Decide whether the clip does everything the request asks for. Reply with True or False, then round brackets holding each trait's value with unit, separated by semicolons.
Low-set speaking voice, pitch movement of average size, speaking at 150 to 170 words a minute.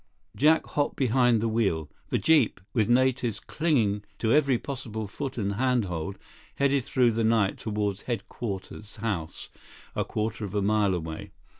True (110 Hz; 4.1 semitones; 155 wpm)